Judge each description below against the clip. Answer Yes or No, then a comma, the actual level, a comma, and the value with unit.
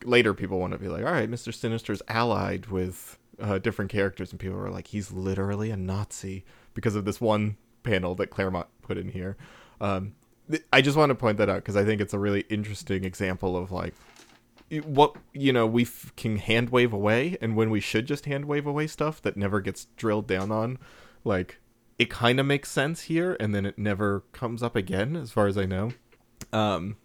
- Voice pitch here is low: Yes, low, 110 Hz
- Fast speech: Yes, fast, 215 wpm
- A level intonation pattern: No, average, 3.5 semitones